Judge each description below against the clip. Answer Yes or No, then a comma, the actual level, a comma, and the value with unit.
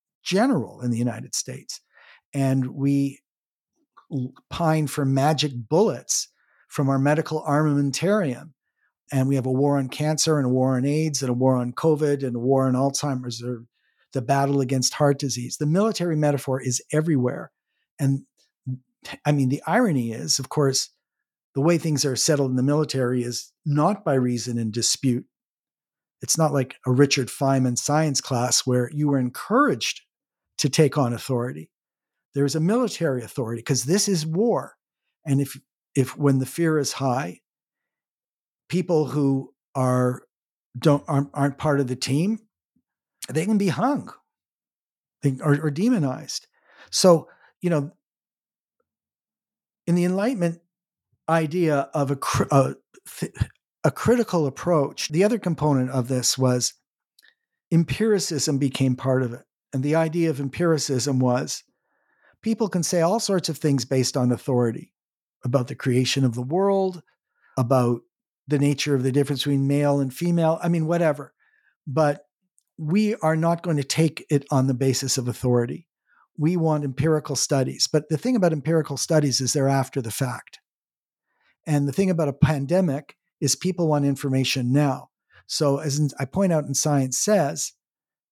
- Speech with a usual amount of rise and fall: Yes, average, 3.6 semitones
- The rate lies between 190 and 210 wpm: No, average, 155 wpm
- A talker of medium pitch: Yes, medium, 145 Hz